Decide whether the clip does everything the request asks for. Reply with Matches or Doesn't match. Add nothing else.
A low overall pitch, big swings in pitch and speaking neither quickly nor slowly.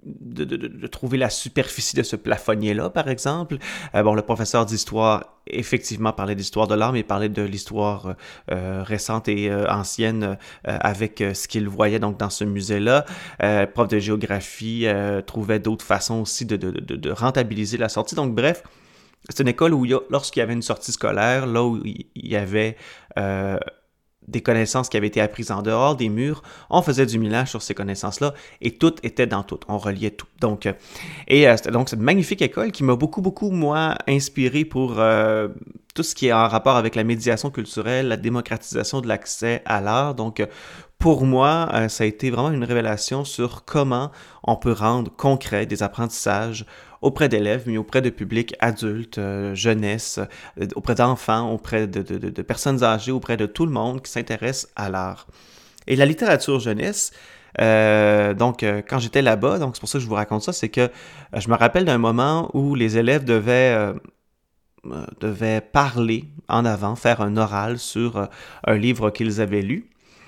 Doesn't match